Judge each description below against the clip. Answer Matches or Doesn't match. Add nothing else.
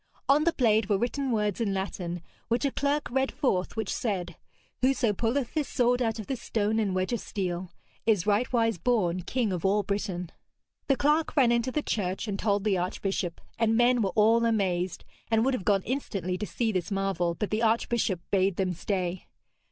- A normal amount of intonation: Matches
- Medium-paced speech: Matches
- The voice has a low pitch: Doesn't match